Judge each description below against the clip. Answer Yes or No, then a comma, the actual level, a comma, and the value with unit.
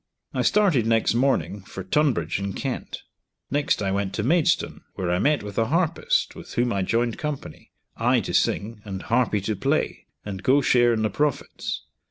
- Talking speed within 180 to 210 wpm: Yes, average, 185 wpm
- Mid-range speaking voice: No, low, 115 Hz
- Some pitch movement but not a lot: No, wide, 5.8 semitones